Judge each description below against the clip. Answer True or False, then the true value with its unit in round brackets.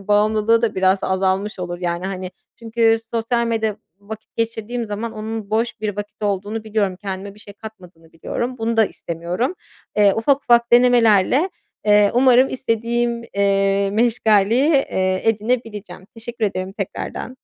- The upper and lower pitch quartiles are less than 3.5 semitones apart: True (2.8 semitones)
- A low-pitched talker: False (215 Hz)